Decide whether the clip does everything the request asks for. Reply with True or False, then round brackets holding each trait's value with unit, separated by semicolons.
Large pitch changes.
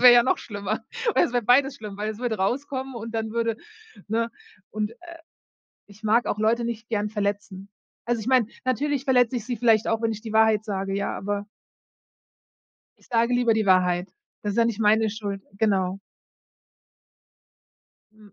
False (2.5 semitones)